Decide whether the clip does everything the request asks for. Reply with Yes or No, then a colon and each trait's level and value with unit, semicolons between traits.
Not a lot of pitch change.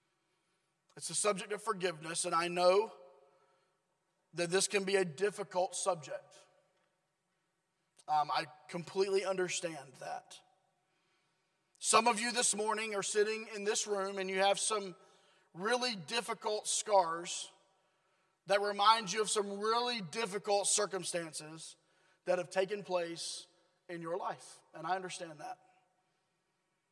Yes: narrow, 1.4 semitones